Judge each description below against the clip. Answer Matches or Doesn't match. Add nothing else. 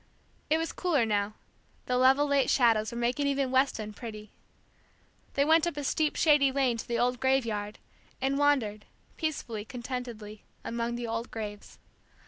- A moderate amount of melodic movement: Matches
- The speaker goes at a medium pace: Matches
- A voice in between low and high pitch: Doesn't match